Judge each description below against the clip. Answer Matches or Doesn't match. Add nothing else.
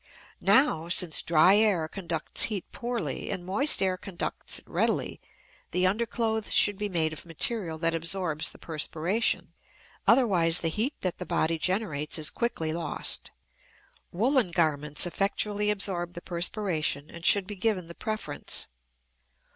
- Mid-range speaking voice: Matches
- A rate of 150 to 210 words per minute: Doesn't match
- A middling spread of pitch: Matches